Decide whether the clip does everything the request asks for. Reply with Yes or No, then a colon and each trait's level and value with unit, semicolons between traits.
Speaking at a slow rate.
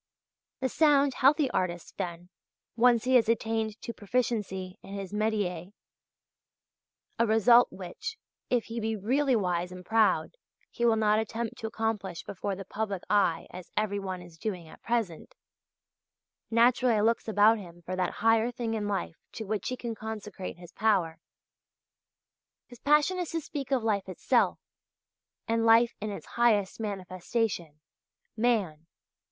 No: average, 150 wpm